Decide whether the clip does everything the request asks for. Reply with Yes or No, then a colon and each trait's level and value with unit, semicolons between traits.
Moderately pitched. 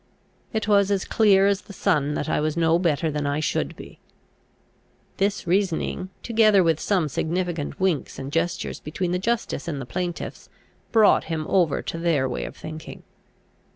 Yes: medium, 175 Hz